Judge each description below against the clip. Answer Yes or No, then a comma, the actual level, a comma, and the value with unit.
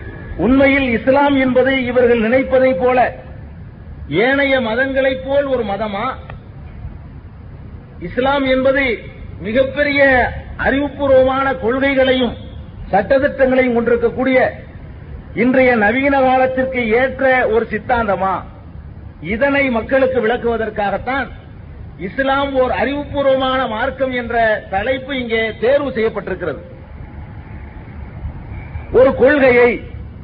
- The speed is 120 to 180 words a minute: No, slow, 75 wpm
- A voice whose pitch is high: Yes, very high, 250 Hz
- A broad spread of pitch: No, average, 4.8 semitones